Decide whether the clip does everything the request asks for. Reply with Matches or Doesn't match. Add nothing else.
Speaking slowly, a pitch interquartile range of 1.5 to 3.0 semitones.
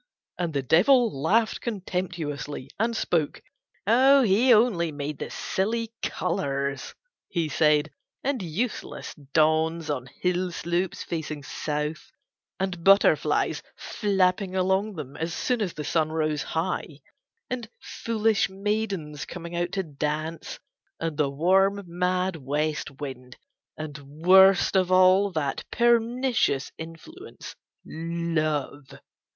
Doesn't match